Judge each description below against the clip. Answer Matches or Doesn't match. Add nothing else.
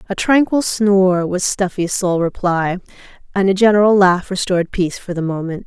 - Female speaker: Matches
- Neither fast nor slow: Matches